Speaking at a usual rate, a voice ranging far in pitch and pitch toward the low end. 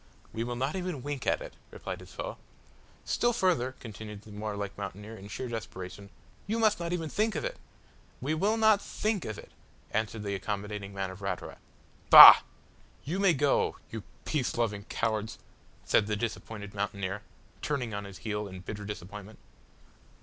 Yes: average, 170 wpm; wide, 6.7 semitones; low, 110 Hz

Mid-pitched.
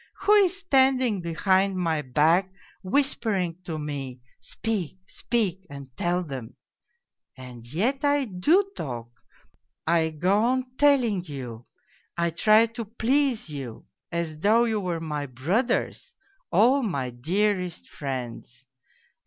Yes: medium, 180 Hz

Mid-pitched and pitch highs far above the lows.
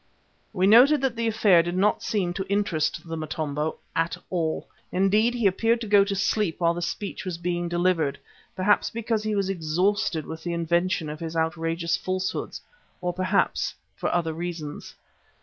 No: medium, 180 Hz; average, 3.7 semitones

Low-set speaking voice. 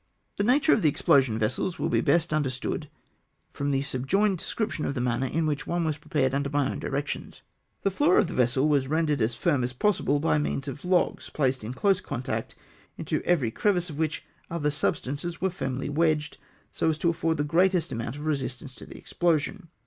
No: medium, 150 Hz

